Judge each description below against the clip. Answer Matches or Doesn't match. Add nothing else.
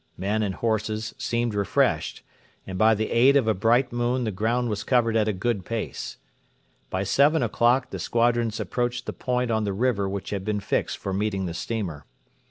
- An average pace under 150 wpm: Doesn't match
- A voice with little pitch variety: Doesn't match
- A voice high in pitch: Doesn't match